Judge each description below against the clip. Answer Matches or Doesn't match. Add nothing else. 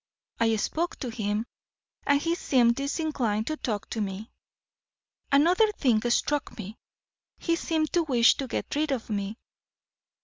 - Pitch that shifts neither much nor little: Doesn't match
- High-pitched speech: Matches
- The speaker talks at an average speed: Matches